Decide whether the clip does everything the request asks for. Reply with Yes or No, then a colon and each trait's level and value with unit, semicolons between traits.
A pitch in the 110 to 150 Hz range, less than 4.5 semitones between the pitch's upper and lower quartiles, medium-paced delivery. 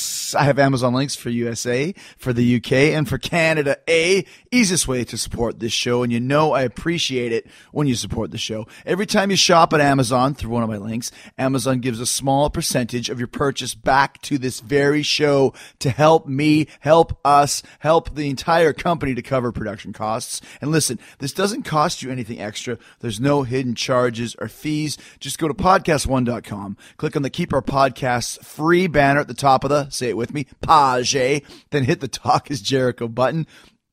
Yes: low, 135 Hz; average, 3.7 semitones; average, 195 wpm